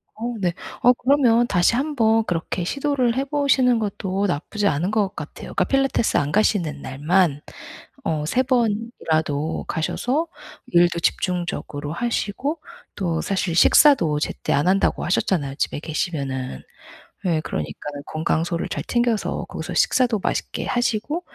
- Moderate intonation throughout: No, wide, 7.1 semitones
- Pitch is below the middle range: No, high, 190 Hz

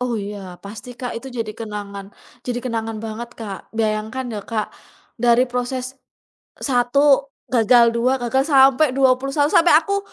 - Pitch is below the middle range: No, high, 245 Hz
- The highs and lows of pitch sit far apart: No, average, 3.1 semitones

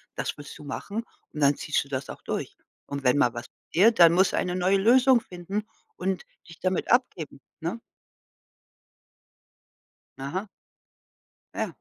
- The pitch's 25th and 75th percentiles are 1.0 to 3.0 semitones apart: No, wide, 5.7 semitones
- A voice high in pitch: No, medium, 180 Hz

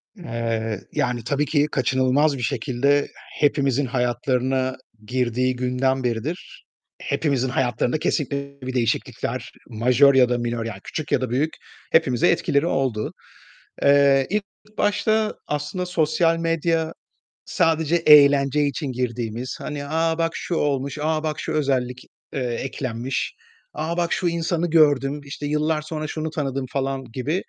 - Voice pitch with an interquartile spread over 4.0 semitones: No, average, 3.6 semitones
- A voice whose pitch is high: No, medium, 140 Hz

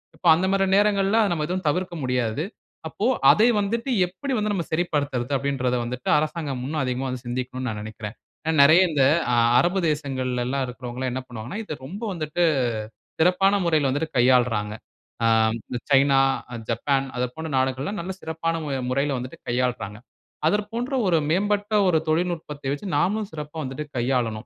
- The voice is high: No, medium, 145 Hz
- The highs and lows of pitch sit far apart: Yes, wide, 5.9 semitones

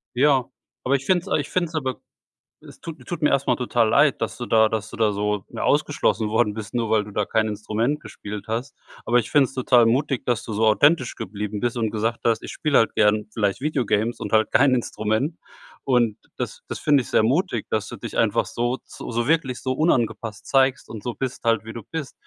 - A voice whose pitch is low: Yes, low, 120 Hz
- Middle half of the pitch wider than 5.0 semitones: No, average, 3.6 semitones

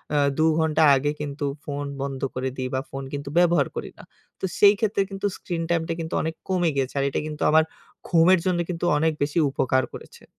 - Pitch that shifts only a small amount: No, average, 3.5 semitones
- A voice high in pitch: No, medium, 160 Hz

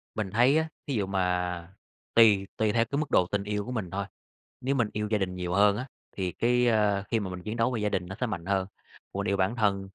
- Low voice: Yes, low, 100 Hz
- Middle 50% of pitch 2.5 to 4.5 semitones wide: Yes, average, 3.2 semitones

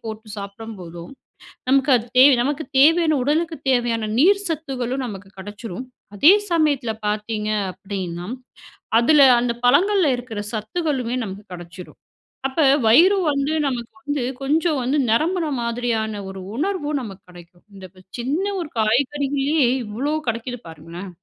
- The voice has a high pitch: Yes, high, 245 Hz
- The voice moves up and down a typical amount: No, wide, 5.8 semitones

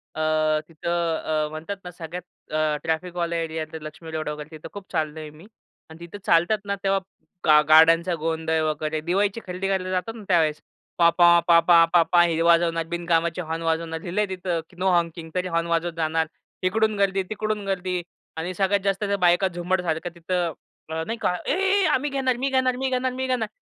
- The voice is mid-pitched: Yes, medium, 170 Hz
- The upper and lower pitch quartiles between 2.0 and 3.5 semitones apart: Yes, average, 2.9 semitones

